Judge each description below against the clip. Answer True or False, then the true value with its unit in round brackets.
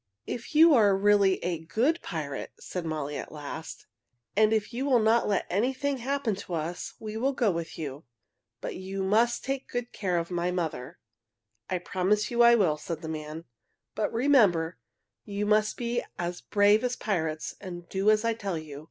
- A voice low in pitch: False (200 Hz)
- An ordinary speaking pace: True (185 wpm)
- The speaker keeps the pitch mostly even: False (5.6 semitones)